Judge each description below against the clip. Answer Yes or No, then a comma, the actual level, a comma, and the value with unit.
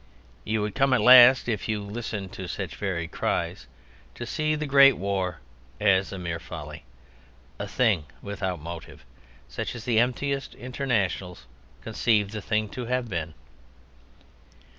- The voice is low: Yes, low, 105 Hz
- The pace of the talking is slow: No, average, 145 wpm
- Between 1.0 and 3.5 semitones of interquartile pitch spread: No, average, 4.9 semitones